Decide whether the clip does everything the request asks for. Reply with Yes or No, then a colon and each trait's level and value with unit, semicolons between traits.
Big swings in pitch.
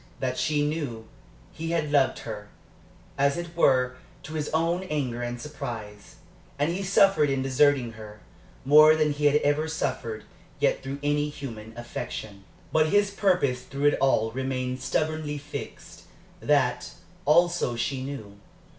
No: average, 3.9 semitones